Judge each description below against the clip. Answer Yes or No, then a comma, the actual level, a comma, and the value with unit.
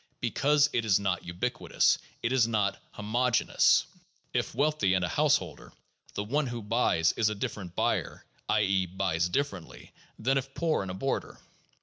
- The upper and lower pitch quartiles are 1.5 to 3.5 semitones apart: No, wide, 5.4 semitones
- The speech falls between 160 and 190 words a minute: Yes, average, 175 wpm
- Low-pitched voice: Yes, low, 110 Hz